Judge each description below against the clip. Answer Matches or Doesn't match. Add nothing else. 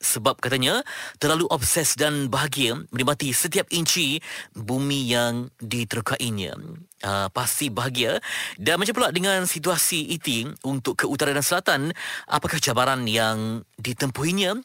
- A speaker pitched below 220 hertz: Matches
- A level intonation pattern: Doesn't match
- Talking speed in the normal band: Matches